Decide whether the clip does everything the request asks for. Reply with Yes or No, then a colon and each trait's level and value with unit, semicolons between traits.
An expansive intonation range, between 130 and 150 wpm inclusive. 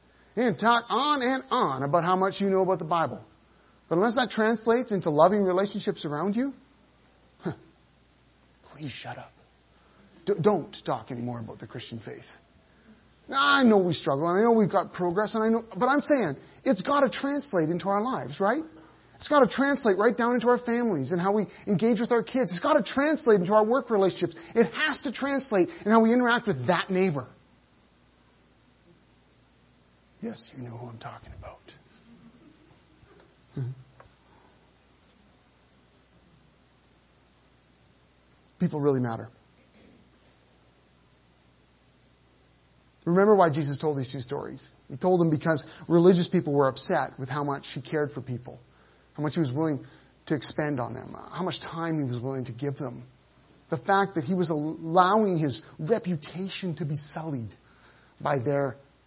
No: wide, 7.8 semitones; average, 160 wpm